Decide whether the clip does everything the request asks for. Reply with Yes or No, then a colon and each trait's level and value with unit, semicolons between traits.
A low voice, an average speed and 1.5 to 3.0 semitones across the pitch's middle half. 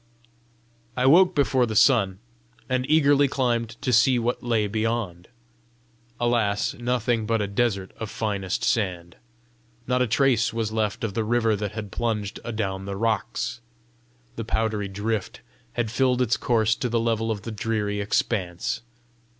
Yes: low, 115 Hz; average, 150 wpm; average, 2.7 semitones